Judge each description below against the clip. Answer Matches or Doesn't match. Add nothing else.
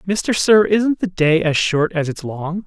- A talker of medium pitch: Matches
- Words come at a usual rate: Doesn't match